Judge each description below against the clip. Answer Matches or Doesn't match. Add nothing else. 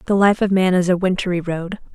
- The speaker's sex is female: Matches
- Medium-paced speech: Doesn't match